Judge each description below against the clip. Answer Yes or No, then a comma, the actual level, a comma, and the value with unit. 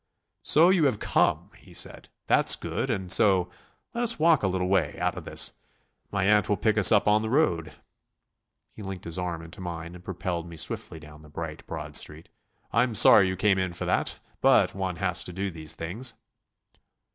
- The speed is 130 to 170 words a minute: No, average, 200 wpm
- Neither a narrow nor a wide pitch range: Yes, average, 3.8 semitones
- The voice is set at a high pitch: No, very low, 95 Hz